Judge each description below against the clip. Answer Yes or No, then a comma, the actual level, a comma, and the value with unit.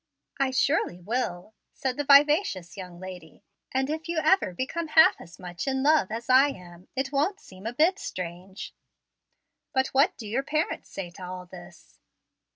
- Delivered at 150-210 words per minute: Yes, average, 170 wpm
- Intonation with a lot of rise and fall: Yes, wide, 8.1 semitones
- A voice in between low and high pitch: No, very high, 255 Hz